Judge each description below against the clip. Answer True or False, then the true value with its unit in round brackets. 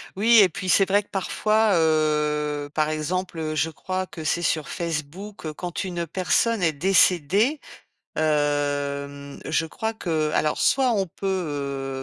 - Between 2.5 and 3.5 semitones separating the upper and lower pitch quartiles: False (4.1 semitones)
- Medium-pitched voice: True (165 Hz)